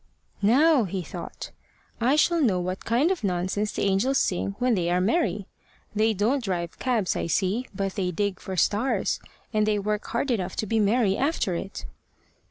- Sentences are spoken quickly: No, average, 180 wpm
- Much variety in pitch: No, average, 4.6 semitones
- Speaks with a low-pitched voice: No, high, 210 Hz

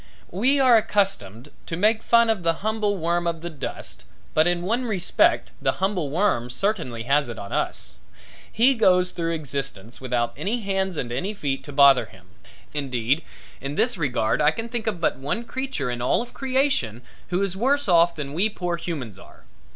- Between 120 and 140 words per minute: No, average, 185 wpm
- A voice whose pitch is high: No, medium, 170 Hz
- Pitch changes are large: Yes, wide, 7.5 semitones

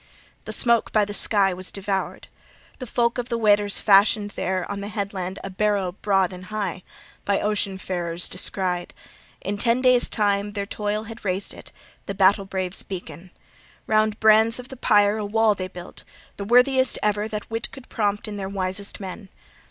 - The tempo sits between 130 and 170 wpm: No, average, 185 wpm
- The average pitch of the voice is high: Yes, high, 205 Hz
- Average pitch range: No, narrow, 2.1 semitones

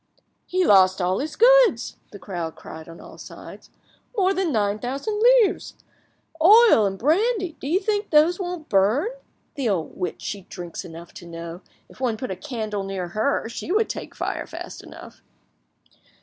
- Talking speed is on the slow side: No, average, 170 wpm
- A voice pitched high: Yes, high, 245 Hz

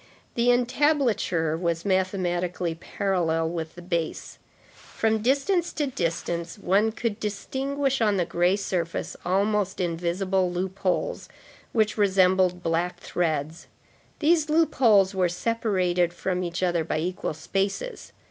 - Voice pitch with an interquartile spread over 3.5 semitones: Yes, average, 4.1 semitones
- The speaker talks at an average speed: No, slow, 120 wpm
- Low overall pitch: No, medium, 185 Hz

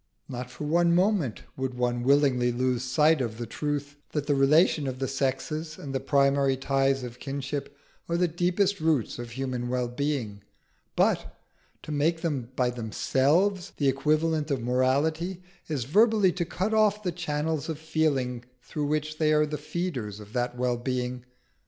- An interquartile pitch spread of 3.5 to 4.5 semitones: Yes, average, 4.0 semitones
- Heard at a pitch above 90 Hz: Yes, medium, 140 Hz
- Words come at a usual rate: Yes, average, 165 wpm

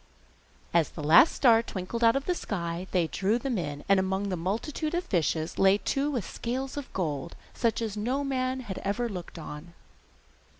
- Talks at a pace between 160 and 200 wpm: Yes, average, 185 wpm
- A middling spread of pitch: No, wide, 6.8 semitones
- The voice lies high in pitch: Yes, high, 205 Hz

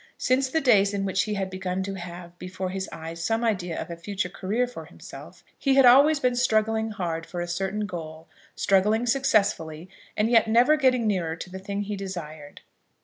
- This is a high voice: Yes, high, 195 Hz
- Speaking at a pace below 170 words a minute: No, average, 200 wpm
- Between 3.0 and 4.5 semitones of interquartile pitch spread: Yes, average, 4.2 semitones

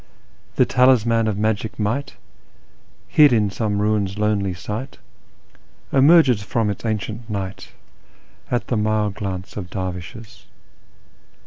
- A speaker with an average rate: No, slow, 125 wpm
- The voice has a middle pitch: No, low, 105 Hz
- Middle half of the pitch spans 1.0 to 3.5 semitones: Yes, narrow, 2.6 semitones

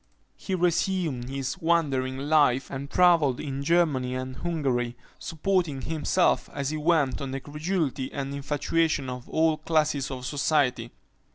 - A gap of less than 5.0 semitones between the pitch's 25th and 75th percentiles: Yes, average, 3.6 semitones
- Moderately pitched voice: Yes, medium, 145 Hz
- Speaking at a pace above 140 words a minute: No, slow, 135 wpm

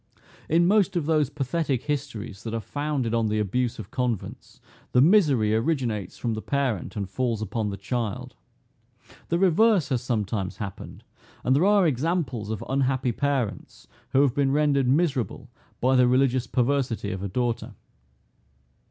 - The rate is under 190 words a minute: Yes, average, 155 wpm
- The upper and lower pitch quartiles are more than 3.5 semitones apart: Yes, average, 4.5 semitones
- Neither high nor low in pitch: No, low, 125 Hz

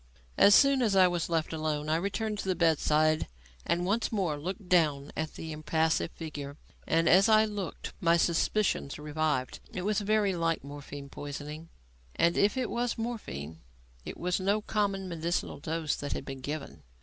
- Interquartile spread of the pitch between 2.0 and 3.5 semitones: No, average, 4.6 semitones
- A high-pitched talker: No, medium, 165 Hz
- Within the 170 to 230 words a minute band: Yes, average, 175 wpm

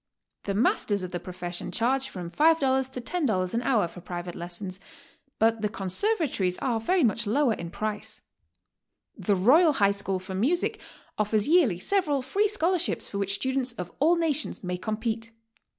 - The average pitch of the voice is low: No, high, 225 Hz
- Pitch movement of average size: No, wide, 7.0 semitones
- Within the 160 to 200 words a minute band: Yes, average, 165 wpm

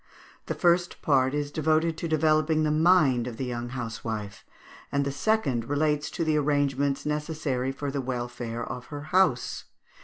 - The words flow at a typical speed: Yes, average, 160 wpm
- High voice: No, medium, 145 Hz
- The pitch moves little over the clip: No, average, 3.8 semitones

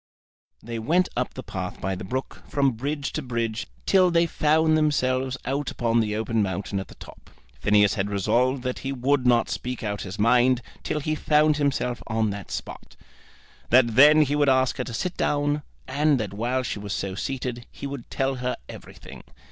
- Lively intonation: No, average, 4.3 semitones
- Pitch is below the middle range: Yes, low, 125 Hz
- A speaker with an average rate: Yes, average, 195 wpm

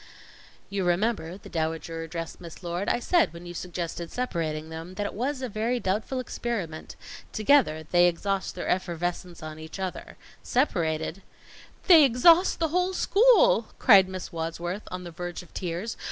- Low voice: No, medium, 180 Hz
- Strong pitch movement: Yes, wide, 6.2 semitones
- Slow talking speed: No, average, 165 wpm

